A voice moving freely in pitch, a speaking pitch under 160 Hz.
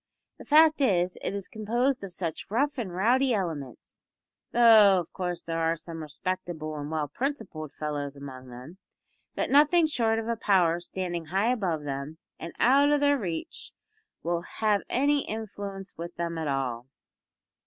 No: wide, 6.4 semitones; medium, 185 Hz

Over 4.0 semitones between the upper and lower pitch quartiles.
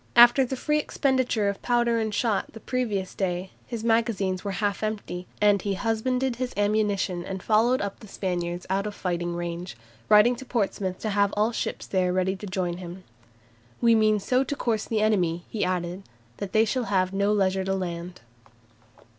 No: average, 3.5 semitones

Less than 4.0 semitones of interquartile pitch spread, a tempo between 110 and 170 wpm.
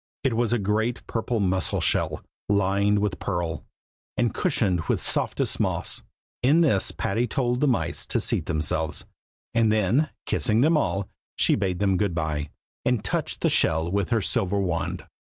No: average, 4.5 semitones; average, 165 wpm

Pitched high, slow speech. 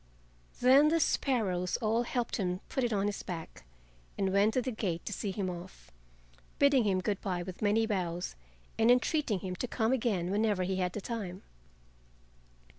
No: high, 205 Hz; average, 180 wpm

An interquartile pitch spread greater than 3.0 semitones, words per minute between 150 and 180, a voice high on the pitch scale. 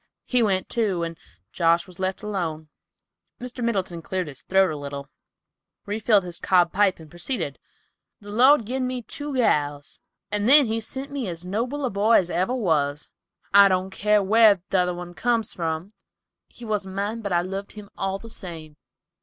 Yes: average, 4.6 semitones; average, 175 wpm; high, 195 Hz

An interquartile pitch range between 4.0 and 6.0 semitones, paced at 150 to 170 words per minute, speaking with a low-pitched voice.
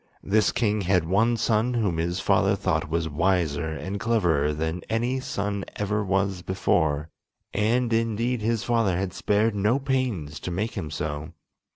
Yes: average, 5.1 semitones; average, 160 wpm; low, 100 Hz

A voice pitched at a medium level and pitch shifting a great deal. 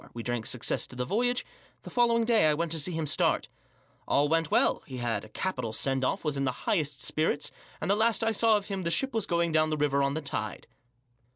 Yes: medium, 155 Hz; wide, 6.8 semitones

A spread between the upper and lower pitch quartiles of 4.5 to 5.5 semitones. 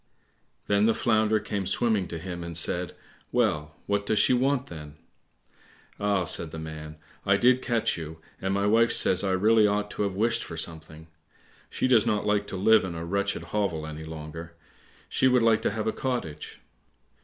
Yes: average, 5.0 semitones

